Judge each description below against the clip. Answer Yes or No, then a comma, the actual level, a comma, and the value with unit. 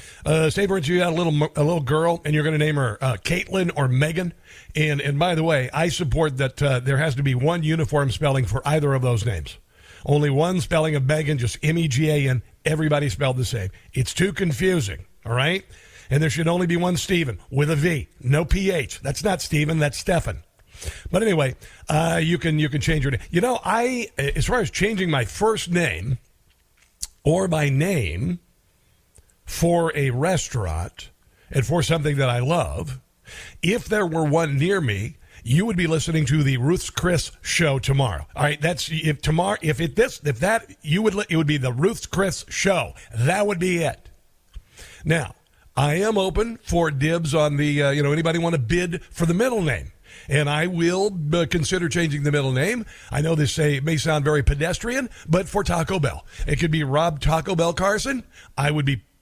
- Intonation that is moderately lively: Yes, average, 4.0 semitones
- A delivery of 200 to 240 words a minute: Yes, fast, 205 wpm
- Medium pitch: Yes, medium, 155 Hz